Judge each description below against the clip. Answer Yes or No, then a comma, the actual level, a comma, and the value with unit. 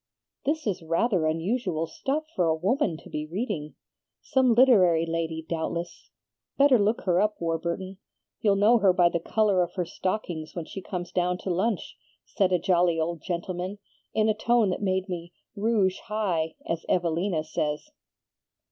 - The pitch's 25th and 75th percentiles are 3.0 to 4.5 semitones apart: Yes, average, 4.0 semitones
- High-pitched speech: No, medium, 180 Hz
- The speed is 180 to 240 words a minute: No, average, 165 wpm